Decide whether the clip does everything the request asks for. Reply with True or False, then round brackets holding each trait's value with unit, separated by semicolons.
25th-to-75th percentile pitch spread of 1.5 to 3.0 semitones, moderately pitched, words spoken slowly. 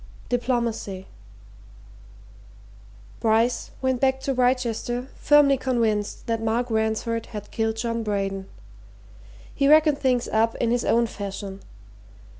False (2.5 semitones; 230 Hz; 110 wpm)